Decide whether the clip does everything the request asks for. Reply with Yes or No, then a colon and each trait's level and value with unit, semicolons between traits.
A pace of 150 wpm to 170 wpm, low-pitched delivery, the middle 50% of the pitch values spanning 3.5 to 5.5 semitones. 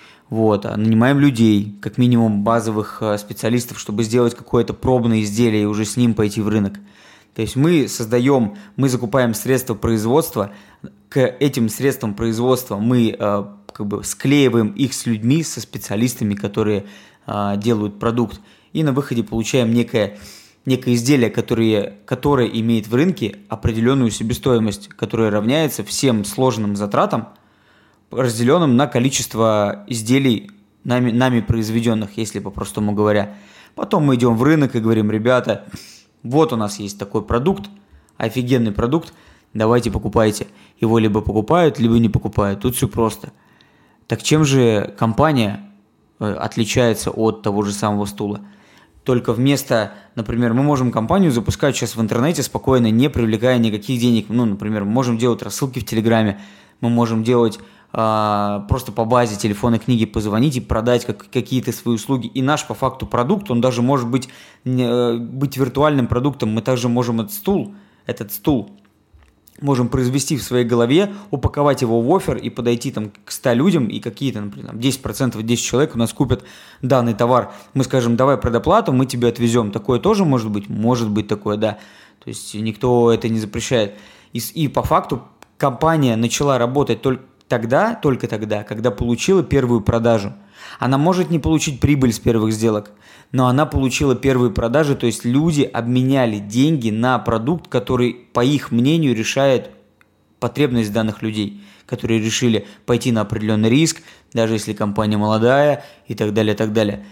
No: average, 155 wpm; low, 120 Hz; average, 3.1 semitones